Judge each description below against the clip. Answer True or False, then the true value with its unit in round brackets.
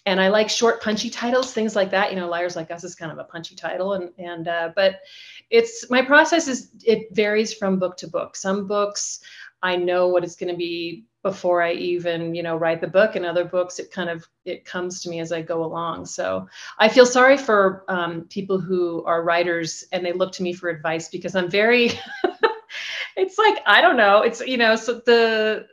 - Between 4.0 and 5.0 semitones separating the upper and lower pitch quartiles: True (4.3 semitones)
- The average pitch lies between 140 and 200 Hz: True (185 Hz)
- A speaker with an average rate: False (220 wpm)